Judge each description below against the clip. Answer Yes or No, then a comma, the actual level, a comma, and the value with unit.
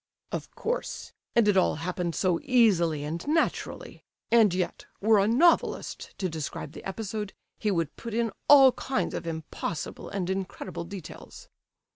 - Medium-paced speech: Yes, average, 150 wpm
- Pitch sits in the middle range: No, high, 195 Hz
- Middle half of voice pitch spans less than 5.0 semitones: No, average, 5.3 semitones